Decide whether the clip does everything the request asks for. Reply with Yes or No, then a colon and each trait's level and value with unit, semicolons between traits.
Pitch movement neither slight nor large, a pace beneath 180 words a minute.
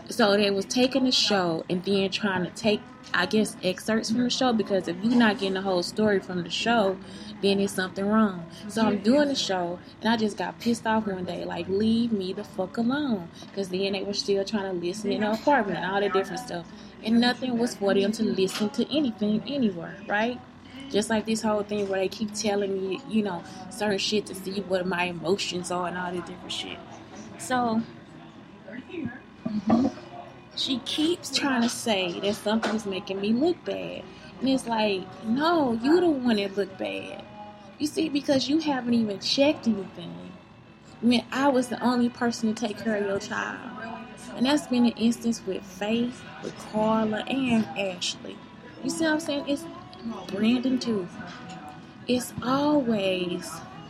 No: average, 3.7 semitones; average, 185 wpm